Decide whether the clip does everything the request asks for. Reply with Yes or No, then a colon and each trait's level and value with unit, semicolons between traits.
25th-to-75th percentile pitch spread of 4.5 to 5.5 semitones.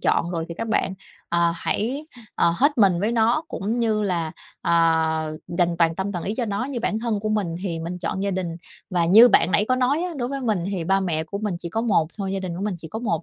Yes: average, 4.8 semitones